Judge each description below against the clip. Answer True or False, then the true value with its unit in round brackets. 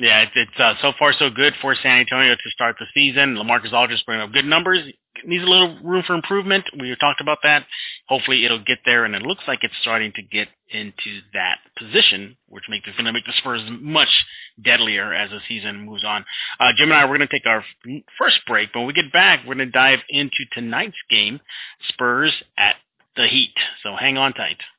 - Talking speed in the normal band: False (225 wpm)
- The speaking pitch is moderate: False (130 Hz)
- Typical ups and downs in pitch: True (3.8 semitones)